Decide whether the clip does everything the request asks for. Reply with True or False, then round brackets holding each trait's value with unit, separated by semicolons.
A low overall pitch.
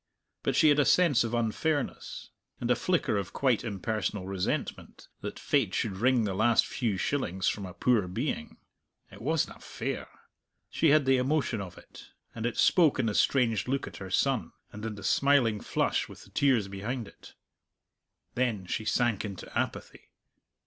True (115 Hz)